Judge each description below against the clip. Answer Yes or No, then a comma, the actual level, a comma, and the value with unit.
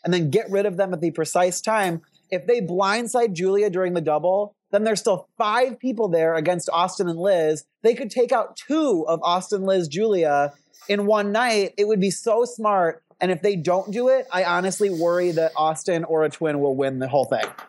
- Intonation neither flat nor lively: Yes, average, 3.9 semitones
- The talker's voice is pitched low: No, medium, 185 Hz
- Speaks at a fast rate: Yes, fast, 215 wpm